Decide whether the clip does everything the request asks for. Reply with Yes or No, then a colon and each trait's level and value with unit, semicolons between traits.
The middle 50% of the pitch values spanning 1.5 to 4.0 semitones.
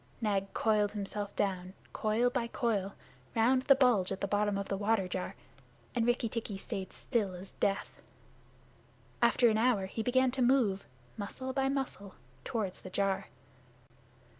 Yes: average, 3.7 semitones